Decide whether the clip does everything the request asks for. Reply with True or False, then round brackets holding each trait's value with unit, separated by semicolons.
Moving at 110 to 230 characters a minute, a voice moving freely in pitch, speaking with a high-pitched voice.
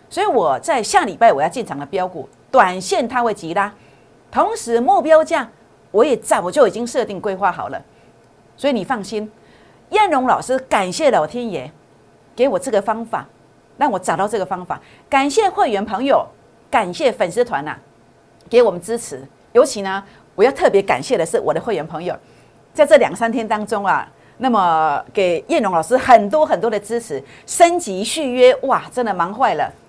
False (265 characters per minute; 6.7 semitones; 245 Hz)